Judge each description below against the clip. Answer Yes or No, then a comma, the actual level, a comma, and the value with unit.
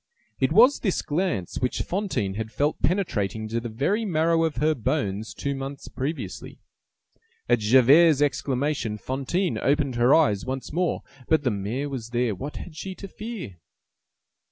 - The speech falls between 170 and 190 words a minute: No, average, 155 wpm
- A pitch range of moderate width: No, wide, 5.8 semitones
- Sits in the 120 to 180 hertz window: Yes, low, 135 Hz